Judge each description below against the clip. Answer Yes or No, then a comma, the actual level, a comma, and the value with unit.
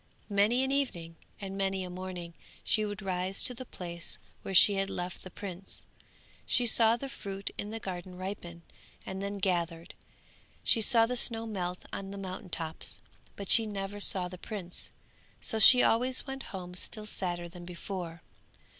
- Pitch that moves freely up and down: No, average, 3.2 semitones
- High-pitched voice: Yes, high, 195 Hz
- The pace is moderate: Yes, average, 170 wpm